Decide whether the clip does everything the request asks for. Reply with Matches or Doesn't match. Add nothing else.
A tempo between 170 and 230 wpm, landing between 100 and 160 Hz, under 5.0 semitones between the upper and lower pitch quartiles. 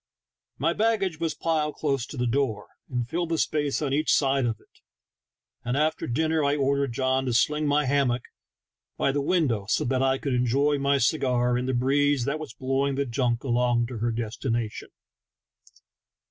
Matches